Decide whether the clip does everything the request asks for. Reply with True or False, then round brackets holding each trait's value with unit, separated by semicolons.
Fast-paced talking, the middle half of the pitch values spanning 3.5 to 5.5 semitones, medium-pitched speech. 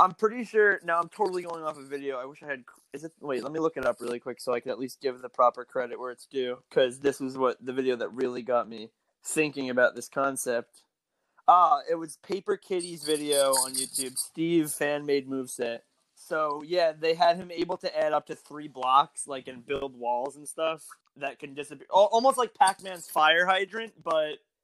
True (220 wpm; 4.6 semitones; 145 Hz)